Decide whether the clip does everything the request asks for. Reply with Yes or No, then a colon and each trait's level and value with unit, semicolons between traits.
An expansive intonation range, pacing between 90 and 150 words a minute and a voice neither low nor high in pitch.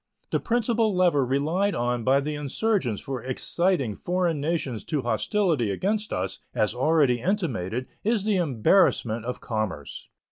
Yes: wide, 7.6 semitones; average, 140 wpm; medium, 145 Hz